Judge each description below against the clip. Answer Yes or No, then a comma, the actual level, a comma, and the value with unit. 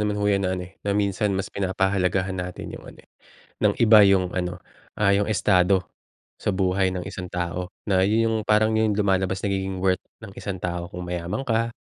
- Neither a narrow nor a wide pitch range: No, narrow, 2.0 semitones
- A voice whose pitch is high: No, very low, 95 Hz